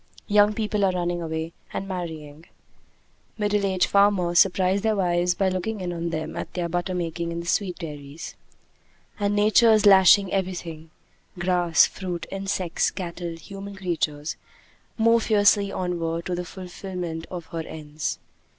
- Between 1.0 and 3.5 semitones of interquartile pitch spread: Yes, average, 2.8 semitones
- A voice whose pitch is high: No, medium, 180 Hz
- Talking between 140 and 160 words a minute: Yes, average, 150 wpm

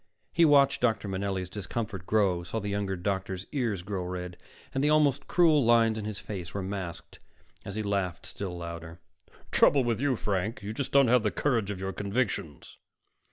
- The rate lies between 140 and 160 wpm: No, average, 185 wpm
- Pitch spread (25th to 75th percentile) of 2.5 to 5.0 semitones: Yes, average, 4.2 semitones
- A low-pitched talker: Yes, low, 100 Hz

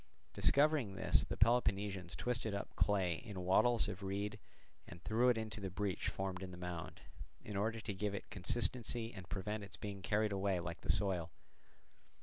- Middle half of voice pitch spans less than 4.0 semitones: Yes, average, 2.7 semitones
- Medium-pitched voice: No, low, 100 Hz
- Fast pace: No, average, 175 wpm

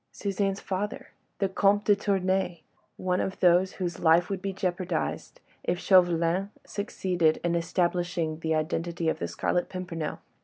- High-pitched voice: No, medium, 180 Hz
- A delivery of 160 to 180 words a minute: No, average, 140 wpm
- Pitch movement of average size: No, narrow, 2.1 semitones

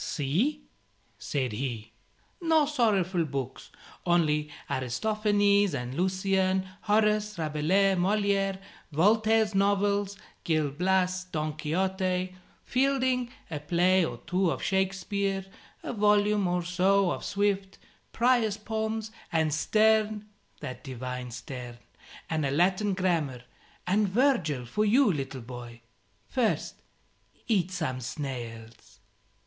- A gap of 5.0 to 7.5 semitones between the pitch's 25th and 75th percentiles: Yes, wide, 5.6 semitones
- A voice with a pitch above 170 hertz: Yes, medium, 185 Hz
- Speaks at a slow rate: Yes, slow, 110 wpm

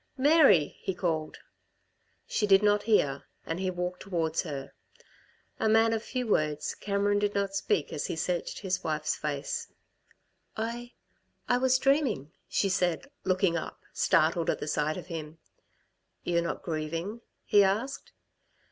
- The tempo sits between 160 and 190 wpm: No, average, 145 wpm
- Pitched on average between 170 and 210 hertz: Yes, medium, 185 Hz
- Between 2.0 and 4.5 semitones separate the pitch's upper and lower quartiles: No, average, 5.0 semitones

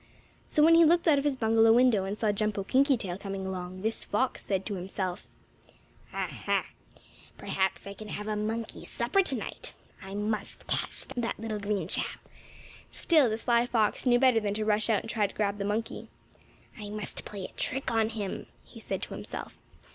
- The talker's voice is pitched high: Yes, high, 215 Hz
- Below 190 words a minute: No, average, 195 wpm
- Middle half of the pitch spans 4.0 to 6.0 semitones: No, average, 3.0 semitones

